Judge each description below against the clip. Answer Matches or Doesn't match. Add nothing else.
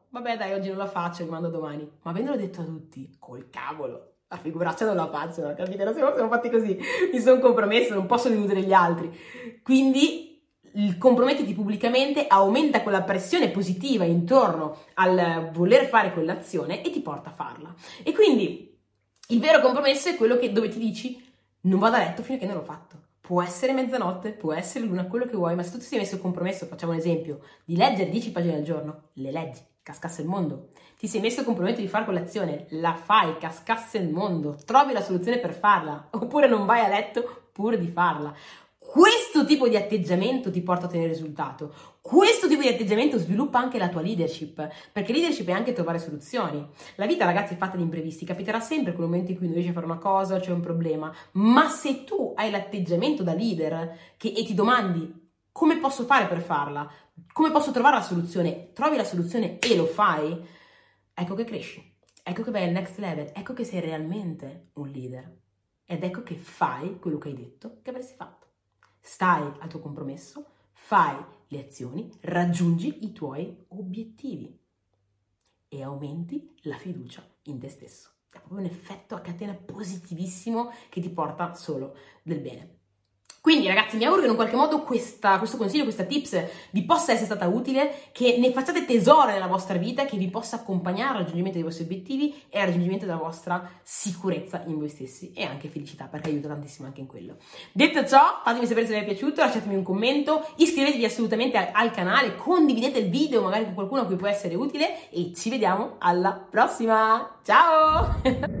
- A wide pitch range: Matches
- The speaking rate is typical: Doesn't match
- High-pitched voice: Matches